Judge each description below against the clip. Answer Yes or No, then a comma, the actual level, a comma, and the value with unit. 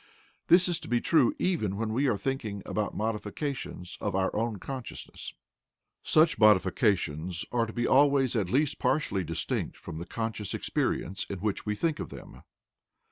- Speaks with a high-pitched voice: No, low, 110 Hz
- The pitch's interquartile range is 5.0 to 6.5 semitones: Yes, wide, 5.6 semitones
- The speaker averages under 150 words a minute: No, average, 165 wpm